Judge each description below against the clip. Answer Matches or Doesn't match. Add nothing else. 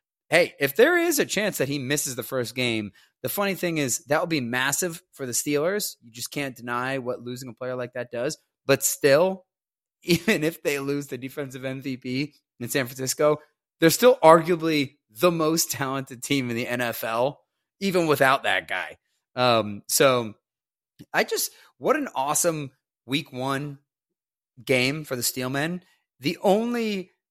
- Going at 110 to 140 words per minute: Doesn't match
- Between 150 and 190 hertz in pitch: Doesn't match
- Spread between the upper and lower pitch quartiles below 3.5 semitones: Doesn't match